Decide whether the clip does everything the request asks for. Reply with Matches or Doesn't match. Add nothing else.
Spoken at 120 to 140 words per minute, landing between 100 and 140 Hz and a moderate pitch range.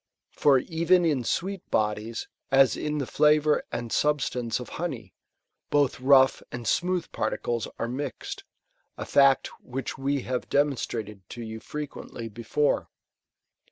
Matches